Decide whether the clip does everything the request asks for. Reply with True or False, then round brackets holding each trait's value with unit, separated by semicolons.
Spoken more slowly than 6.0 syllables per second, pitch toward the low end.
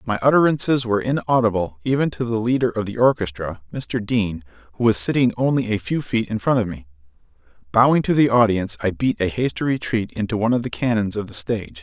False (6.2 syllables/s; 110 Hz)